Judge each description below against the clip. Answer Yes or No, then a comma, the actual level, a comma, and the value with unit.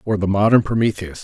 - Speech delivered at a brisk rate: No, average, 195 wpm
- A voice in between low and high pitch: No, low, 100 Hz